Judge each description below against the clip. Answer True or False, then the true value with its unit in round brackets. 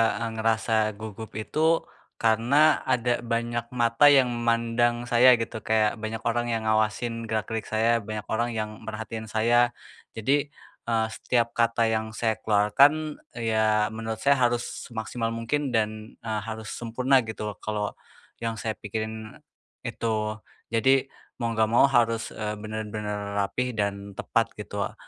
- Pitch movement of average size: False (1.6 semitones)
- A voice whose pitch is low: True (115 Hz)